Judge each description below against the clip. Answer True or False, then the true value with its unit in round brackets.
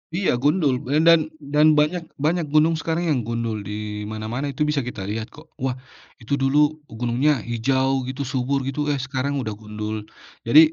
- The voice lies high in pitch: False (135 Hz)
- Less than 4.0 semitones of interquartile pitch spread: False (4.4 semitones)